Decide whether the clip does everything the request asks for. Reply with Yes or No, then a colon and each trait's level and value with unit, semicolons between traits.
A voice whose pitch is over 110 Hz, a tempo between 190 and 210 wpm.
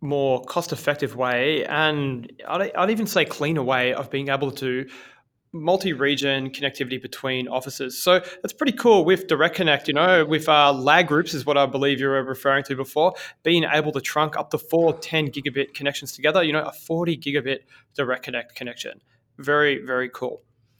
No: medium, 140 Hz; average, 180 wpm